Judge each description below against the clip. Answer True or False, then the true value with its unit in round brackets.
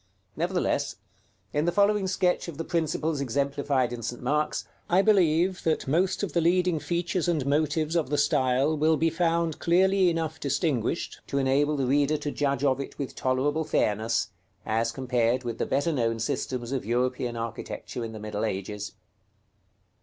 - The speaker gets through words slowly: False (170 wpm)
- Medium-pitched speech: True (145 Hz)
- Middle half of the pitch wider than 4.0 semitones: True (4.8 semitones)